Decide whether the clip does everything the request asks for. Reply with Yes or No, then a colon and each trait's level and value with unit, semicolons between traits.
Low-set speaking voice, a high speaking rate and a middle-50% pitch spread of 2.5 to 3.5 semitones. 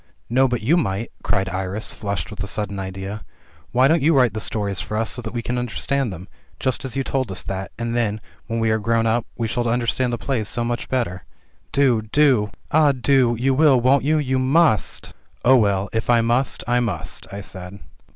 No: low, 120 Hz; fast, 220 wpm; average, 3.9 semitones